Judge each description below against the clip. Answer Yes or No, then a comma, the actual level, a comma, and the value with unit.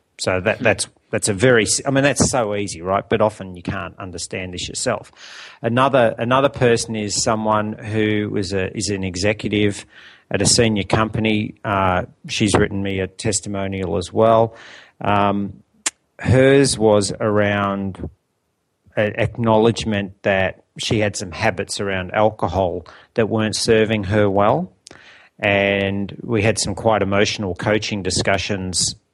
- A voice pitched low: Yes, low, 105 Hz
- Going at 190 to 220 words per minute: No, average, 140 wpm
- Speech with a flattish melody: Yes, narrow, 2.1 semitones